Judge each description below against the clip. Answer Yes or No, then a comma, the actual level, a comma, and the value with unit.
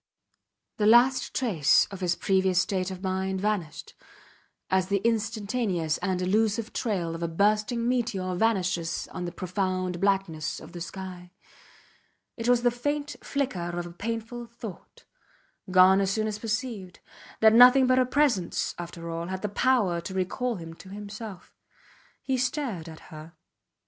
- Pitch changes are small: No, average, 4.4 semitones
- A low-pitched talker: No, high, 195 Hz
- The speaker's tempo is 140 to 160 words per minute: Yes, average, 155 wpm